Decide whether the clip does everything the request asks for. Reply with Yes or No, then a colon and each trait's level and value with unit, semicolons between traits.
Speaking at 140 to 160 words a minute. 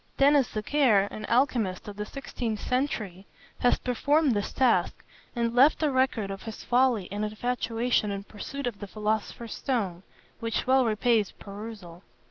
Yes: average, 150 wpm